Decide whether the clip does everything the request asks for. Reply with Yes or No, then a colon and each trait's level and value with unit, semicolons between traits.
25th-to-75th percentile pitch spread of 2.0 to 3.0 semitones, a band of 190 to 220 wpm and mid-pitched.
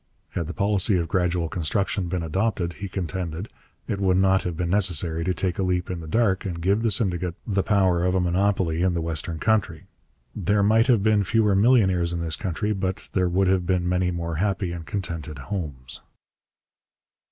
No: narrow, 2.6 semitones; average, 195 wpm; very low, 90 Hz